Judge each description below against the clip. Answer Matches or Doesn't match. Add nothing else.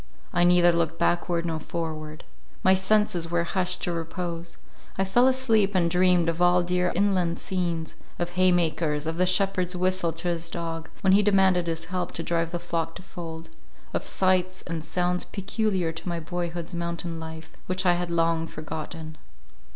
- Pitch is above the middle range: Doesn't match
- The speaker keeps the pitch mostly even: Matches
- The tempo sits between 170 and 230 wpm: Matches